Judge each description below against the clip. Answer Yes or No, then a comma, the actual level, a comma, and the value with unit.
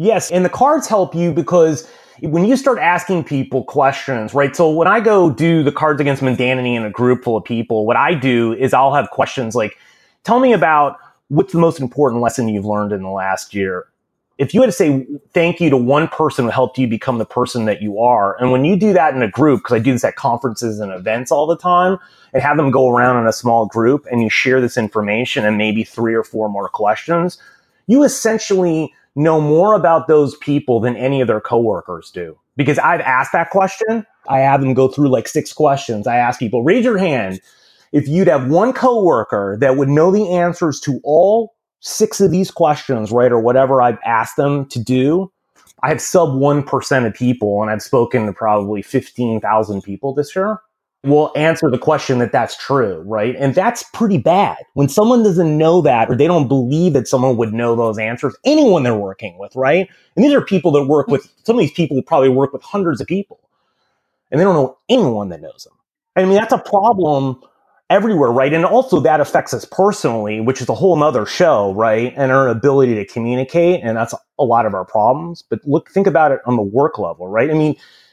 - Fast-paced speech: Yes, fast, 215 wpm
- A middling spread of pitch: No, wide, 6.2 semitones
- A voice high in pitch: No, medium, 140 Hz